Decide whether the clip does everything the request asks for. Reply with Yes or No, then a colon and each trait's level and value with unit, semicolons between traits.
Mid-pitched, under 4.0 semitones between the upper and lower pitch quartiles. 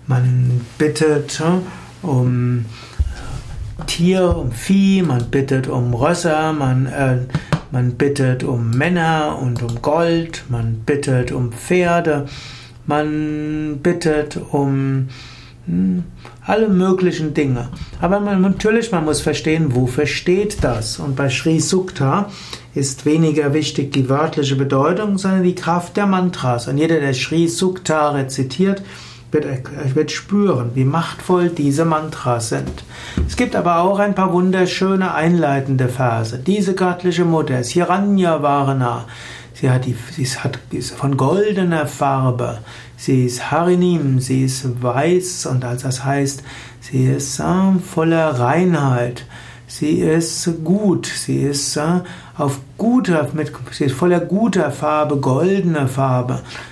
No: medium, 150 Hz; average, 5.0 semitones